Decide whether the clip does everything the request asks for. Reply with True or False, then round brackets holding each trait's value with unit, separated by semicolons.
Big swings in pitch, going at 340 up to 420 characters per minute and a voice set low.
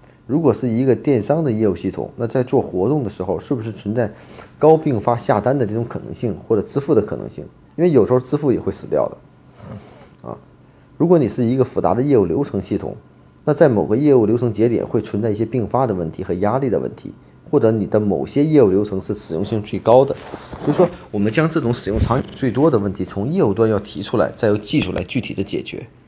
False (4.4 semitones; 345 characters per minute; 115 Hz)